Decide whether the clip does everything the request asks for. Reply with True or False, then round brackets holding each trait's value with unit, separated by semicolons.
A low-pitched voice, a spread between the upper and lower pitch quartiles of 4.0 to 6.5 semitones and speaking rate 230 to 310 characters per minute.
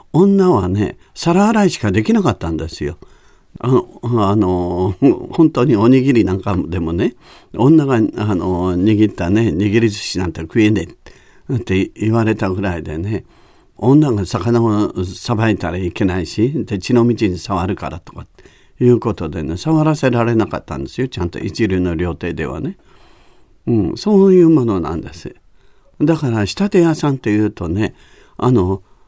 True (105 Hz; 5.3 semitones; 305 characters per minute)